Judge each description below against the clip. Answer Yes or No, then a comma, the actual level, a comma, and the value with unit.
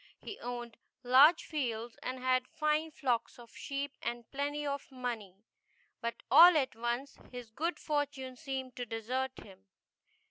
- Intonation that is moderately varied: Yes, average, 3.1 semitones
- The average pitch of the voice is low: No, very high, 255 Hz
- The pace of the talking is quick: No, average, 150 wpm